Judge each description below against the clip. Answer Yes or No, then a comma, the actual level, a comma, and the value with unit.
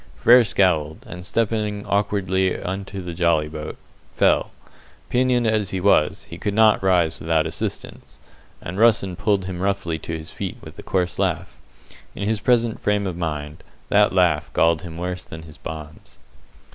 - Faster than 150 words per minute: Yes, average, 165 wpm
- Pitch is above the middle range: No, very low, 95 Hz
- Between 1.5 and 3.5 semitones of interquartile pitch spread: No, average, 3.9 semitones